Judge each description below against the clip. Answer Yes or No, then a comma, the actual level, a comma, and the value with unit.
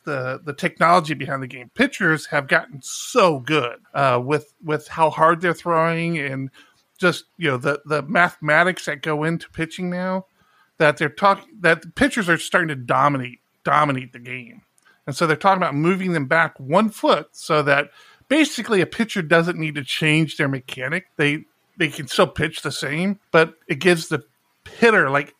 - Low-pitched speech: No, medium, 160 Hz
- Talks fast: No, average, 180 wpm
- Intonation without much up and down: No, average, 3.3 semitones